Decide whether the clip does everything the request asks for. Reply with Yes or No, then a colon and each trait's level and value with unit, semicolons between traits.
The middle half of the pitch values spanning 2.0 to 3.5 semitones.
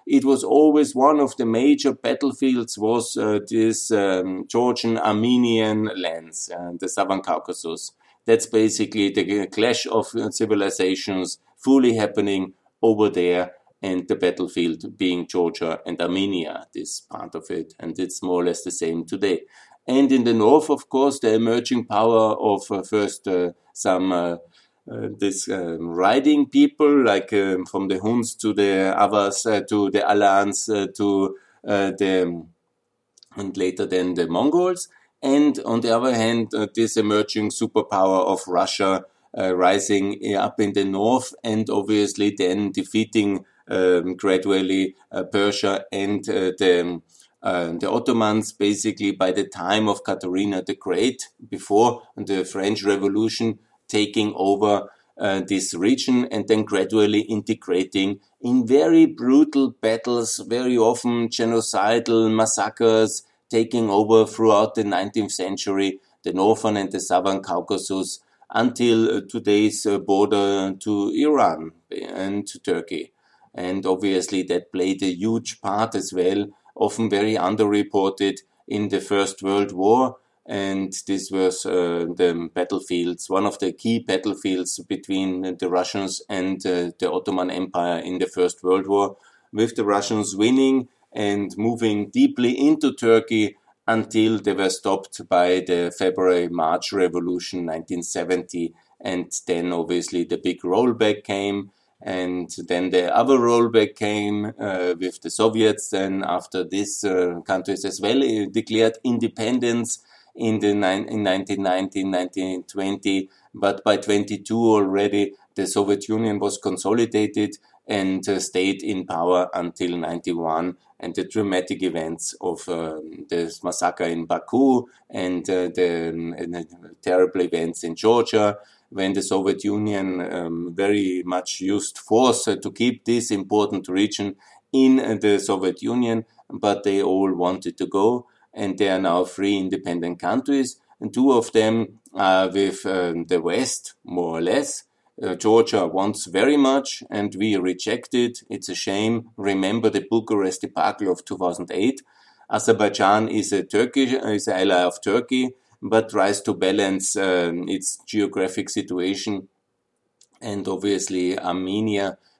Yes: average, 3.2 semitones